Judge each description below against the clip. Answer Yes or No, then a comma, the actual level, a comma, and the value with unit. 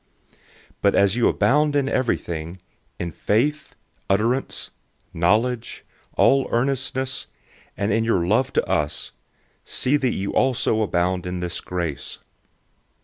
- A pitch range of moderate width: No, wide, 6.5 semitones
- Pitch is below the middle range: Yes, low, 110 Hz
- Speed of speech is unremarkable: No, slow, 125 wpm